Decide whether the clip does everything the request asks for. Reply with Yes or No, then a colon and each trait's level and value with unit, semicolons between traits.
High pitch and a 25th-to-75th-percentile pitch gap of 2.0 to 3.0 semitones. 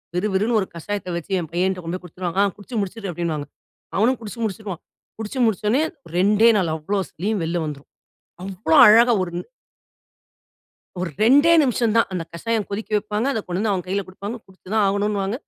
No: high, 200 Hz; average, 3.4 semitones